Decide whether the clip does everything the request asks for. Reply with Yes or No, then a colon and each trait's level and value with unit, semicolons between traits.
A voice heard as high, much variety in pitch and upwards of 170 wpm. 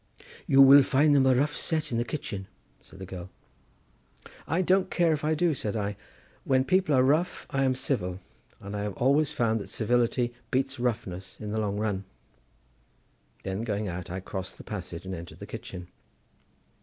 No: low, 120 Hz; wide, 6.3 semitones; average, 185 wpm